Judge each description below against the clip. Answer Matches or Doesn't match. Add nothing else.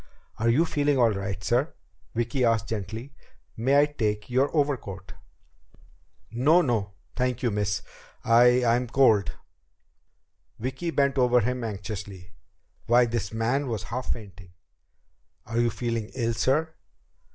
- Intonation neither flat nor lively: Matches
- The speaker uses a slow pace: Matches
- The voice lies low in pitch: Matches